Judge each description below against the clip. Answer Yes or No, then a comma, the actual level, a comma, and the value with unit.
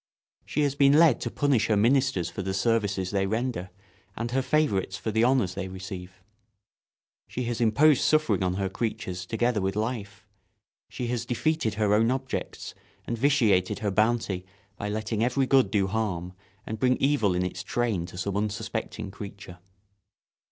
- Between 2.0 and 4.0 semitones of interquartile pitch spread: No, average, 4.5 semitones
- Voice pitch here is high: No, low, 110 Hz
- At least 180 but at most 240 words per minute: No, average, 165 wpm